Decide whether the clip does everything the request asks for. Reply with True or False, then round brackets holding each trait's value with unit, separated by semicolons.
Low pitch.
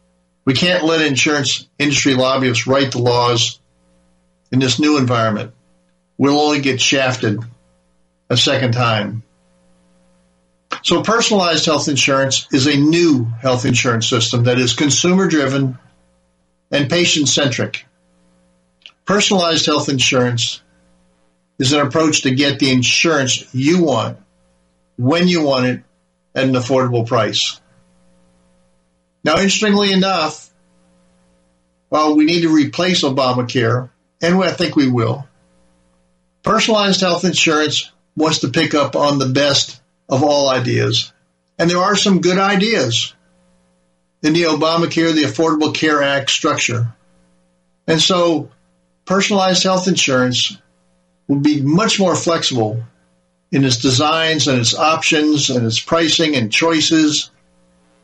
True (130 Hz)